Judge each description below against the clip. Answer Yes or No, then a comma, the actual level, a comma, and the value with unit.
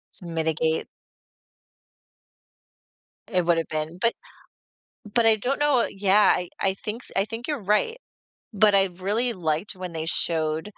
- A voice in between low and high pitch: No, high, 195 Hz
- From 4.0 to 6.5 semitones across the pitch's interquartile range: Yes, average, 5.2 semitones